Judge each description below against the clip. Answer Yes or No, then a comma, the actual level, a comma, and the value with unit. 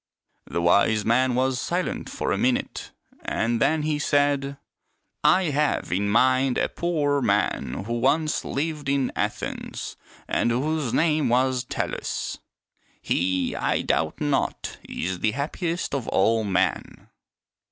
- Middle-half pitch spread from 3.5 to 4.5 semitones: No, average, 5.1 semitones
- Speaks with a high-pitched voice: No, low, 130 Hz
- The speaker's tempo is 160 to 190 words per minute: No, average, 140 wpm